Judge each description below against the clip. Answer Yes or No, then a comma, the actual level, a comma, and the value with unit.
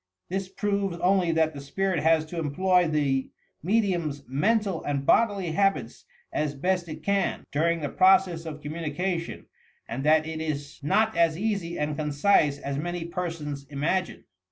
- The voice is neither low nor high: Yes, medium, 165 Hz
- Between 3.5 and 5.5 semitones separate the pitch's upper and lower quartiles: Yes, average, 4.1 semitones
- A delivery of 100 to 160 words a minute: Yes, average, 155 wpm